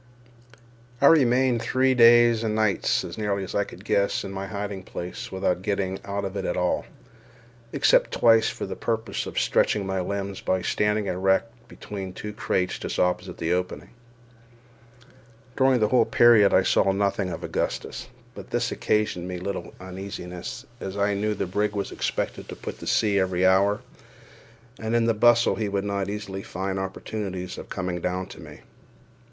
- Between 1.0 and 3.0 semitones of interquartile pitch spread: Yes, narrow, 2.5 semitones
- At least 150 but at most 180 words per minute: Yes, average, 175 wpm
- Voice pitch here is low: Yes, low, 100 Hz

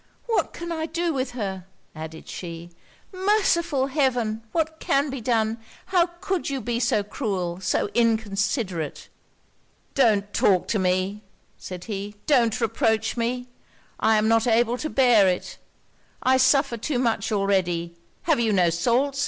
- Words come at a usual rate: Yes, average, 145 wpm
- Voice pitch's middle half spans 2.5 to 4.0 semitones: No, wide, 5.6 semitones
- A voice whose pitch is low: No, high, 230 Hz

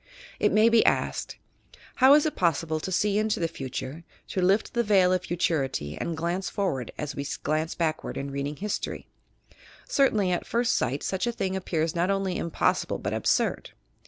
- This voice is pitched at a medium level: Yes, medium, 180 Hz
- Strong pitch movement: No, average, 4.6 semitones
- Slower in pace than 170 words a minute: No, average, 190 wpm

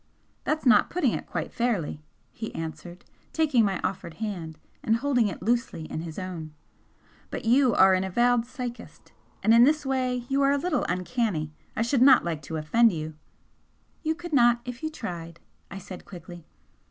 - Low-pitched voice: No, high, 225 Hz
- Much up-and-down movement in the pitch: Yes, wide, 6.6 semitones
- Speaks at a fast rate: No, average, 180 wpm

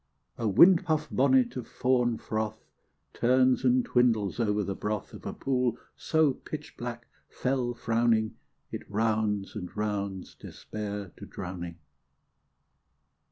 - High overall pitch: No, low, 115 Hz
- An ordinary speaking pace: No, slow, 115 wpm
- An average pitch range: Yes, average, 3.5 semitones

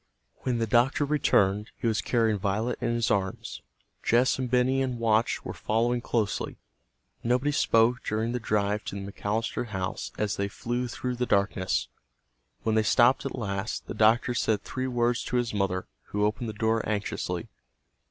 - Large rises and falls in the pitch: No, average, 2.8 semitones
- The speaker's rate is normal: Yes, average, 170 wpm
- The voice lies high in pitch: No, low, 115 Hz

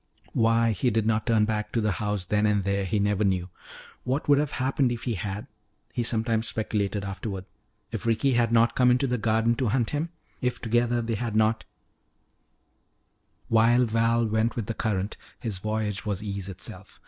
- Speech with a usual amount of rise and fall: No, narrow, 2.2 semitones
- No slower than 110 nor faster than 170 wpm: No, average, 185 wpm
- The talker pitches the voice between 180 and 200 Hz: No, low, 110 Hz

